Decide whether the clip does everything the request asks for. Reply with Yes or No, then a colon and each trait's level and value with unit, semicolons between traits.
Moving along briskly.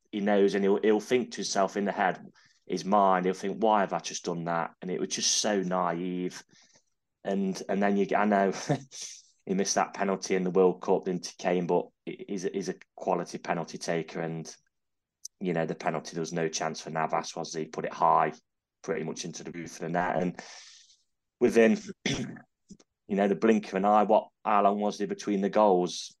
Yes: fast, 215 wpm